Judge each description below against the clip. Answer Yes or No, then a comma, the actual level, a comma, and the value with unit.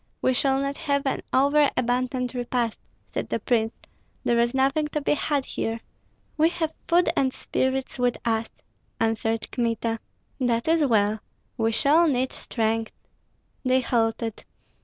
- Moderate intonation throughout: Yes, average, 3.5 semitones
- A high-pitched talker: Yes, very high, 250 Hz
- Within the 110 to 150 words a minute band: Yes, average, 145 wpm